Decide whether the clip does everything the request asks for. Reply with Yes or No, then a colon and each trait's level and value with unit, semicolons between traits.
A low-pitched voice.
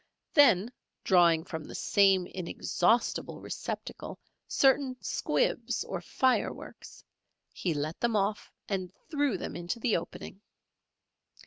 No: high, 195 Hz